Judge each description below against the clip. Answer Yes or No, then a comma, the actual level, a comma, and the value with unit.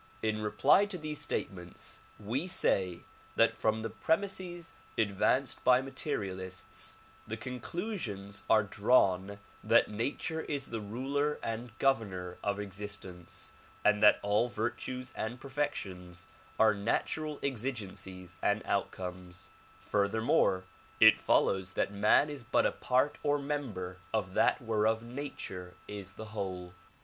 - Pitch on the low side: Yes, low, 110 Hz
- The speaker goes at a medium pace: No, slow, 125 wpm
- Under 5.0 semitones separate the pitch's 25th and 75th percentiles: No, wide, 5.5 semitones